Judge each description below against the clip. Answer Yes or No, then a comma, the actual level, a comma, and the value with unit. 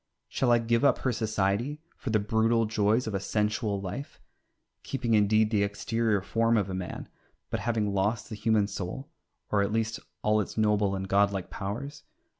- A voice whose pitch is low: Yes, low, 110 Hz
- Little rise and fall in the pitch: Yes, narrow, 2.2 semitones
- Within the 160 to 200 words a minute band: Yes, average, 180 wpm